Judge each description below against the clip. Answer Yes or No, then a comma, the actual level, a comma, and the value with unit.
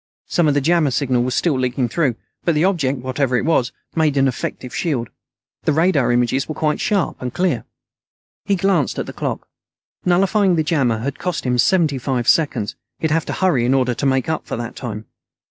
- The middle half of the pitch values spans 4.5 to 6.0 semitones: Yes, average, 4.9 semitones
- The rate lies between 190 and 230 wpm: Yes, fast, 205 wpm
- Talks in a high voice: No, medium, 140 Hz